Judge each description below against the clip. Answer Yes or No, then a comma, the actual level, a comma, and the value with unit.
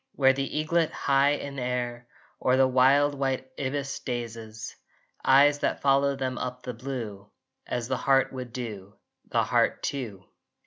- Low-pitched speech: Yes, low, 130 Hz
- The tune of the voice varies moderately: No, narrow, 2.2 semitones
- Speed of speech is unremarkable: Yes, average, 150 wpm